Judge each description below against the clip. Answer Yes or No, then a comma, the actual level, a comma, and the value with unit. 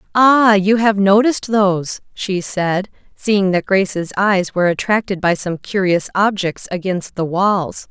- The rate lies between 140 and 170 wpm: Yes, average, 150 wpm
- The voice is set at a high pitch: Yes, high, 195 Hz